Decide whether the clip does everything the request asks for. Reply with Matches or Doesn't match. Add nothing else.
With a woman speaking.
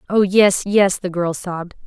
Matches